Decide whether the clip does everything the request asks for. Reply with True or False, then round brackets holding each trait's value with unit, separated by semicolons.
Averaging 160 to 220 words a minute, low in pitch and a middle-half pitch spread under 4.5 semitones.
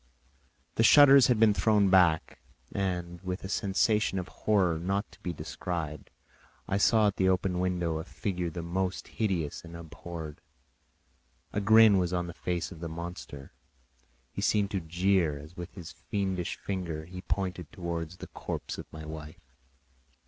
True (165 wpm; 90 Hz; 2.7 semitones)